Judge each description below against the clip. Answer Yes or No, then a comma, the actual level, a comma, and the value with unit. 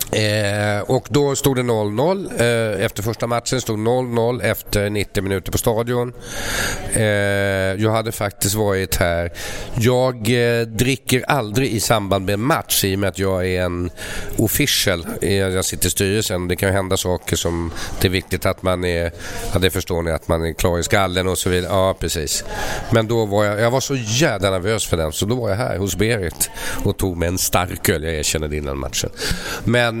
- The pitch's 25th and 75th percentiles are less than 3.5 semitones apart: No, average, 4.1 semitones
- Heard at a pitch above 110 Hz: No, low, 100 Hz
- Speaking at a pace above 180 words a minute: Yes, average, 200 wpm